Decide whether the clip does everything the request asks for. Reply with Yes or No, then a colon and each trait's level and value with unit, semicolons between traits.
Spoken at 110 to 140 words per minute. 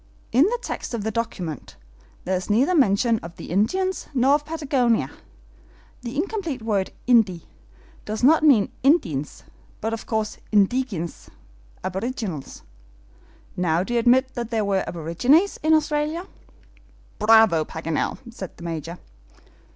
Yes: slow, 135 wpm